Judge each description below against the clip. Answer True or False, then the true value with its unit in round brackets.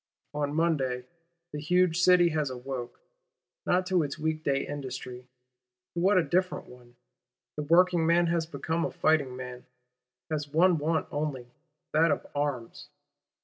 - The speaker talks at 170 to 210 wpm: False (145 wpm)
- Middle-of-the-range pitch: True (155 Hz)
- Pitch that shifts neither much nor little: True (4.1 semitones)